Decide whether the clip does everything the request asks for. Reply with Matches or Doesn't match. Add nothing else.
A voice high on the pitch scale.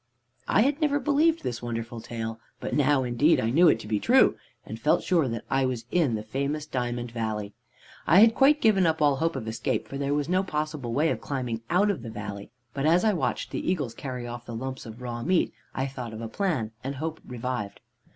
Doesn't match